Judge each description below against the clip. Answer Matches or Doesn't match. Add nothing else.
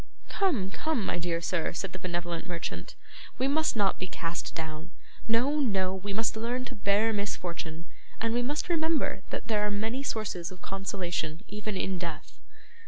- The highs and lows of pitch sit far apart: Doesn't match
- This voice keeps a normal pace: Matches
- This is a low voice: Doesn't match